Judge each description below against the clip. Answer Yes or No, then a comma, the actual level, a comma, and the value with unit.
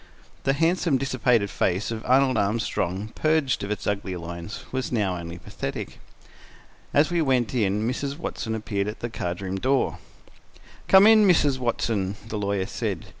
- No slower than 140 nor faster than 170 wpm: Yes, average, 160 wpm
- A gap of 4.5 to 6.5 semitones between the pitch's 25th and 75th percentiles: Yes, wide, 5.5 semitones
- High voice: No, low, 115 Hz